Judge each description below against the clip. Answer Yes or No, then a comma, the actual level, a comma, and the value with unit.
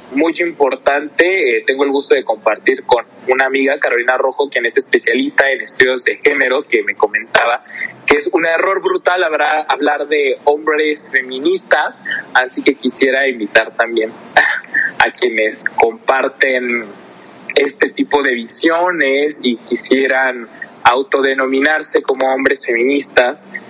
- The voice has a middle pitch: Yes, medium, 150 Hz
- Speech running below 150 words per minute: Yes, slow, 125 wpm